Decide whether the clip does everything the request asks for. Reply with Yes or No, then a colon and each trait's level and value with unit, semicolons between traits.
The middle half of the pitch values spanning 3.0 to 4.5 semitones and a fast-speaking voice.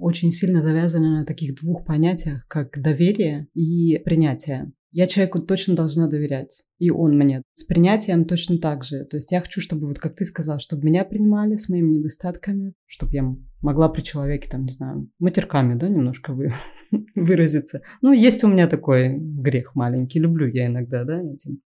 Yes: average, 3.8 semitones; fast, 175 wpm